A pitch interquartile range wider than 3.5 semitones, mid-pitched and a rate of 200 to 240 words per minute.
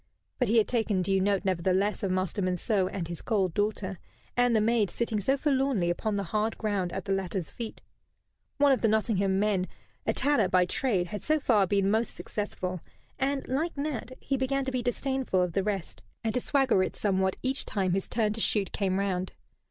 No: average, 4.5 semitones; high, 210 Hz; fast, 205 wpm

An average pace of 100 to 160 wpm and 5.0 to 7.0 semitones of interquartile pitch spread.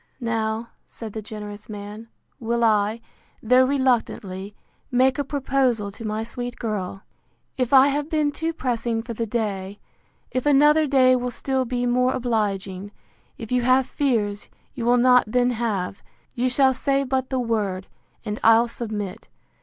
No: average, 155 wpm; average, 3.3 semitones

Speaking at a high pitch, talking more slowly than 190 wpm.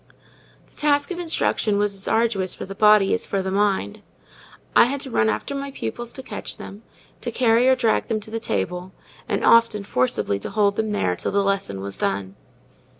No: high, 210 Hz; average, 200 wpm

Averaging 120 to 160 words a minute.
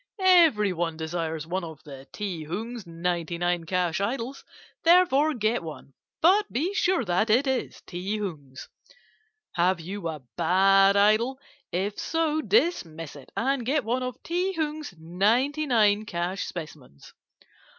Yes: average, 140 wpm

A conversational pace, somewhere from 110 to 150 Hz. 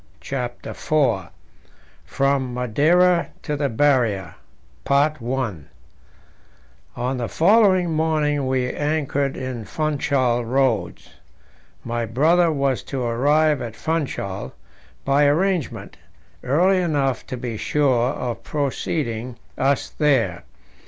No: slow, 100 wpm; low, 135 Hz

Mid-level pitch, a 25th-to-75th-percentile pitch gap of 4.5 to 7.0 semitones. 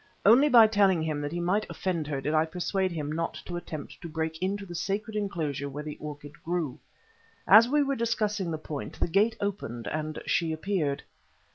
Yes: medium, 170 Hz; average, 4.8 semitones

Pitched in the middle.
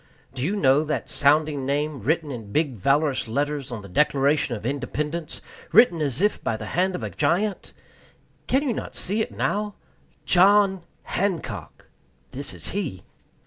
Yes: medium, 150 Hz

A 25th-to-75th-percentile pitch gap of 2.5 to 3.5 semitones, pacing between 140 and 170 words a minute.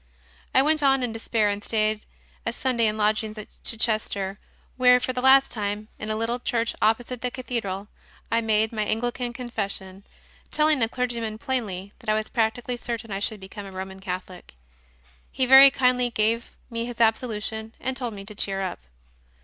No: average, 2.8 semitones; average, 180 wpm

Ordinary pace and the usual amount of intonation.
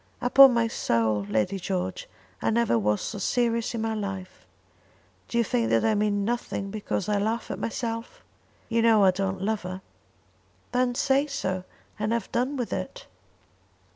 Yes: average, 170 wpm; average, 3.9 semitones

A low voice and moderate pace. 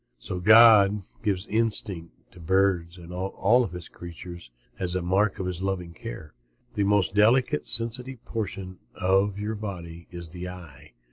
Yes: very low, 95 Hz; average, 150 wpm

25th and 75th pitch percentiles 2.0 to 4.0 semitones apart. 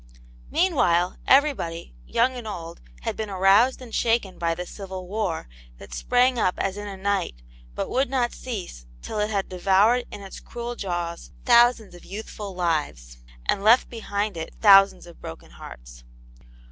No: average, 5.0 semitones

